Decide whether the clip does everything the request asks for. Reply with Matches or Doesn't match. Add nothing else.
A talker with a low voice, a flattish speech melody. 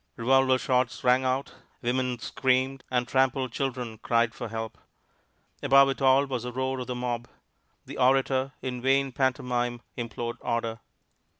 Matches